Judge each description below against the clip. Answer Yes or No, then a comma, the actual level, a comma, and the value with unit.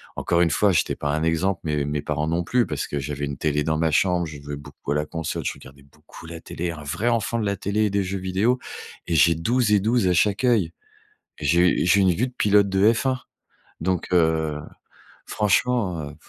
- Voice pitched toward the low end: Yes, very low, 85 Hz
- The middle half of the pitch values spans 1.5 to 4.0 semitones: No, average, 4.9 semitones